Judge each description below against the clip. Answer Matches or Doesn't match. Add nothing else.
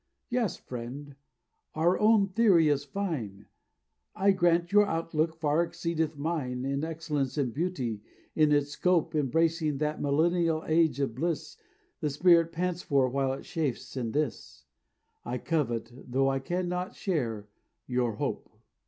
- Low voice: Doesn't match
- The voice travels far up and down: Doesn't match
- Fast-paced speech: Doesn't match